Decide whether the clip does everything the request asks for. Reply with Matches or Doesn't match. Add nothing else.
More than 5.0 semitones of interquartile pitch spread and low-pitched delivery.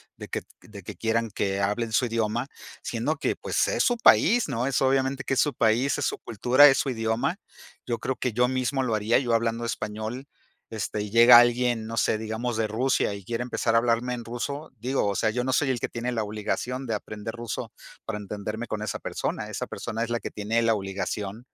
Doesn't match